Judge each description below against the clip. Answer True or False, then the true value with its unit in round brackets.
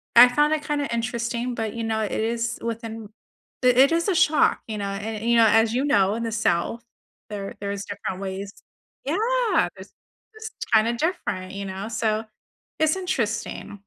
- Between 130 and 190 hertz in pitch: False (230 Hz)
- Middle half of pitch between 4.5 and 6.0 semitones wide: False (3.8 semitones)